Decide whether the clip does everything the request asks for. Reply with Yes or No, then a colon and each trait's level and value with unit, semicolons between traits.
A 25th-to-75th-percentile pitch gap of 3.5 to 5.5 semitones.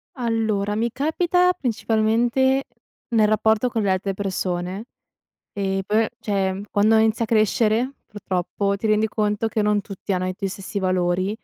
No: narrow, 2.5 semitones